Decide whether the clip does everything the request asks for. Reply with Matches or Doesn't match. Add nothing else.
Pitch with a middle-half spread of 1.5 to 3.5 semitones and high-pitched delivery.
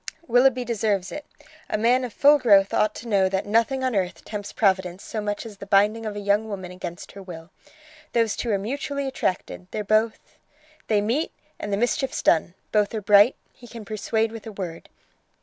Matches